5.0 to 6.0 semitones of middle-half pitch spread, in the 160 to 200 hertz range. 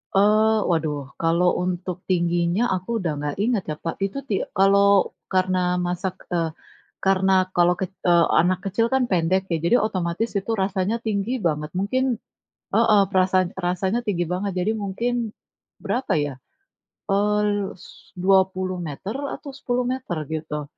No: average, 3.2 semitones; high, 190 Hz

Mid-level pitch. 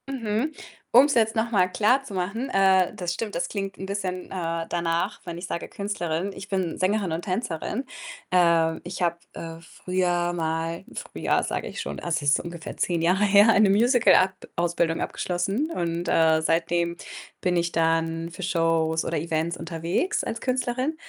Yes: medium, 180 Hz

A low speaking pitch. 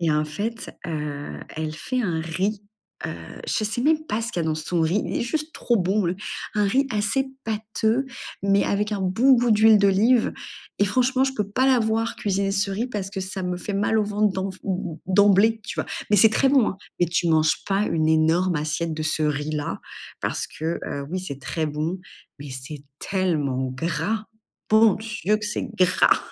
No: high, 195 Hz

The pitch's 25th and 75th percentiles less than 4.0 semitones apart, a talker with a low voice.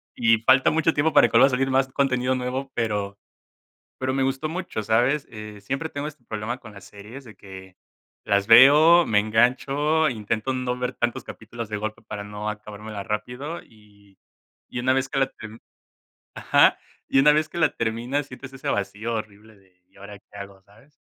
No: average, 4.3 semitones; low, 115 Hz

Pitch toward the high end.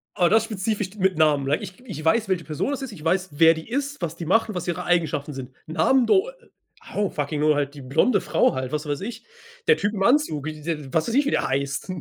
No: medium, 170 Hz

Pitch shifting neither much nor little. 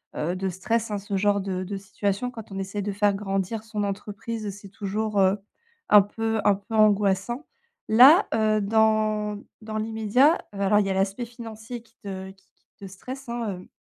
No: narrow, 2.1 semitones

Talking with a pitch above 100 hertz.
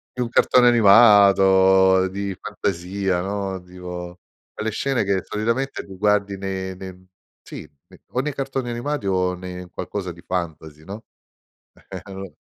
No: very low, 95 Hz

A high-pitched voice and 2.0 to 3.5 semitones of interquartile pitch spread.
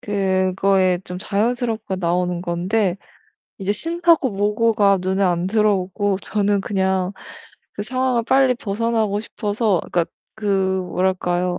Yes: high, 200 Hz; average, 3.0 semitones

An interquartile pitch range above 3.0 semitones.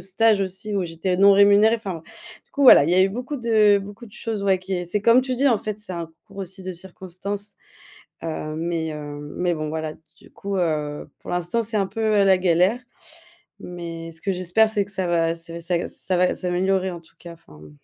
Yes: average, 3.4 semitones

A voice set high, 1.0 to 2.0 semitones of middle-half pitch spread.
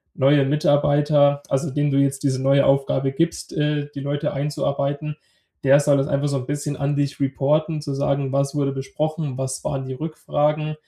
No: medium, 140 Hz; narrow, 1.3 semitones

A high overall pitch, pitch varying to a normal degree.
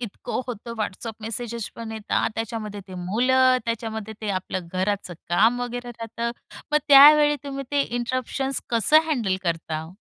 Yes: high, 230 Hz; average, 3.6 semitones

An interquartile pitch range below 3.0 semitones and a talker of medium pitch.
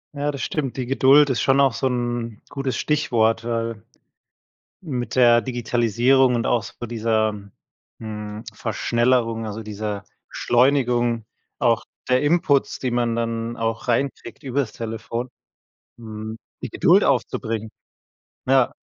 No: narrow, 2.5 semitones; low, 120 Hz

